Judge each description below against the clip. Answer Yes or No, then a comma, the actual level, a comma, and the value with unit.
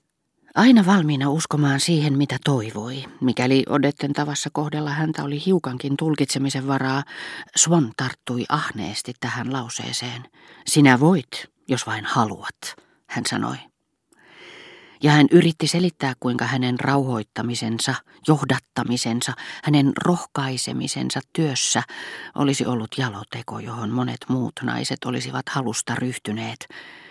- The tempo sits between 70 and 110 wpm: Yes, average, 105 wpm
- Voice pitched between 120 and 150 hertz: Yes, low, 135 Hz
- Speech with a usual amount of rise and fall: Yes, average, 3.3 semitones